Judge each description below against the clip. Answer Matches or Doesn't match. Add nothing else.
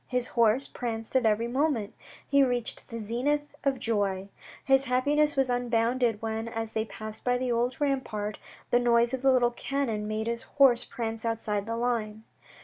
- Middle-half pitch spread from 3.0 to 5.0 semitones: Doesn't match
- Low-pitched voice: Doesn't match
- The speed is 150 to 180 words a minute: Matches